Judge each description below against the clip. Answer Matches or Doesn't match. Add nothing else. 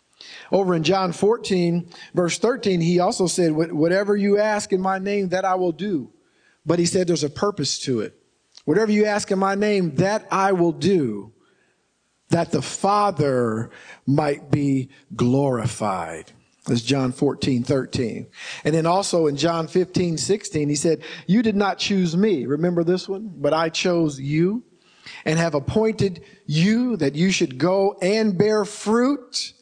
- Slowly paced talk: Doesn't match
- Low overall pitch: Doesn't match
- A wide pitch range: Doesn't match